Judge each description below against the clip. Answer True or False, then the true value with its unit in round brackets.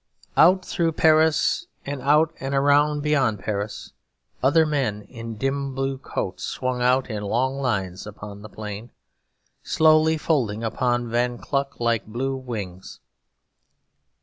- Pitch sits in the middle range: False (130 Hz)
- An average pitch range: True (4.7 semitones)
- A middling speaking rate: False (130 wpm)